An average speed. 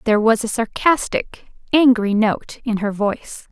Yes: average, 155 wpm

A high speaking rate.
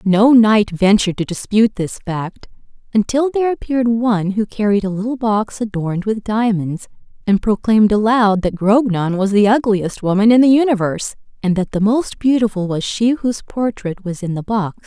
No: average, 180 wpm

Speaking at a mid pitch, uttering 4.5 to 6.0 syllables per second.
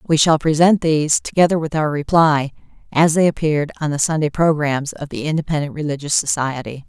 Yes: medium, 155 Hz; 5.8 syllables/s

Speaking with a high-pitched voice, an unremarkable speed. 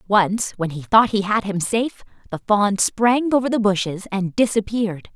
Yes: high, 205 Hz; average, 185 wpm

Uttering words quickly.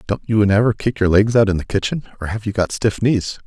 Yes: fast, 275 wpm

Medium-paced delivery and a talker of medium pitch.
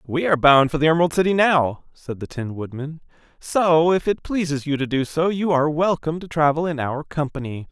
No: fast, 220 wpm; medium, 155 Hz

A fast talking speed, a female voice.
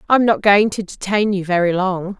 Yes: fast, 220 wpm; female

